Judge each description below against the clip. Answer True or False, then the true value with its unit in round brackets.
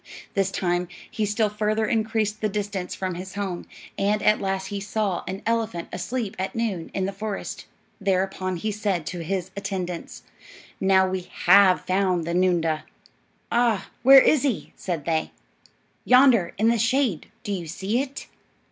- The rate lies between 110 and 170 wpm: True (160 wpm)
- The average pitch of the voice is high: True (195 Hz)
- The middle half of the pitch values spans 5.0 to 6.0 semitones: False (2.9 semitones)